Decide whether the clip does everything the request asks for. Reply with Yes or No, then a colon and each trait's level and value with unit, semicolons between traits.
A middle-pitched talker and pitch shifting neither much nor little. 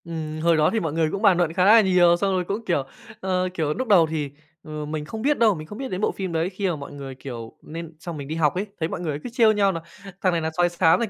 Yes: medium, 170 Hz; average, 3.8 semitones